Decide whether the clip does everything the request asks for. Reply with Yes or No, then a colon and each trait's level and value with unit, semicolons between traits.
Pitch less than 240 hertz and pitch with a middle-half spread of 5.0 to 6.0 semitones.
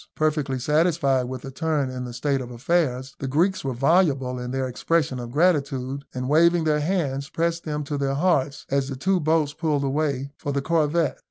No: medium, 140 Hz; average, 3.3 semitones